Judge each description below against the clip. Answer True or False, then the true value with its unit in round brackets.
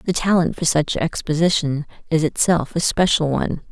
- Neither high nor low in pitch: True (160 Hz)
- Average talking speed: True (160 wpm)